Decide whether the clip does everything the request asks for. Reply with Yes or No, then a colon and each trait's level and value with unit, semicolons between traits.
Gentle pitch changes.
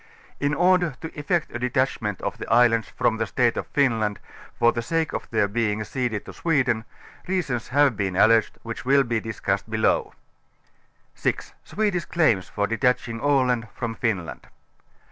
No: average, 4.2 semitones